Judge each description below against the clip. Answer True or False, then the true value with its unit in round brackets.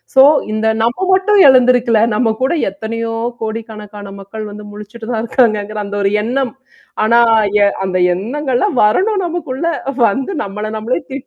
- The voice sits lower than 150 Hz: False (225 Hz)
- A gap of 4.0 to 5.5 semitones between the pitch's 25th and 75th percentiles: False (3.6 semitones)